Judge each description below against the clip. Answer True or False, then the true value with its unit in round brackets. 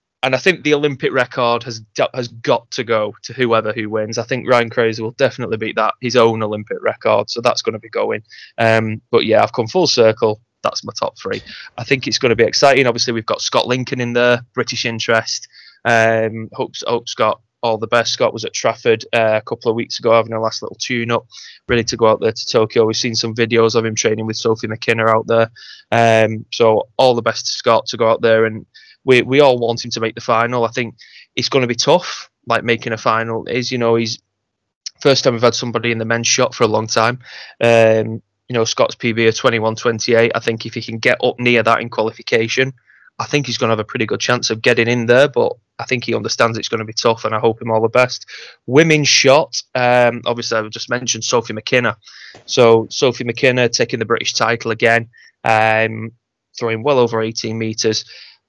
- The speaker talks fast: True (230 wpm)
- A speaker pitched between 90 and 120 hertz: True (115 Hz)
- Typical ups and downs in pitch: False (1.5 semitones)